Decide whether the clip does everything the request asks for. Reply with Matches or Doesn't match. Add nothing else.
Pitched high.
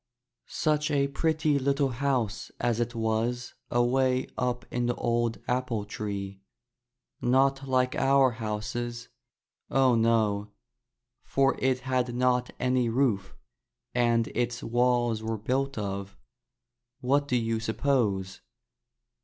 Doesn't match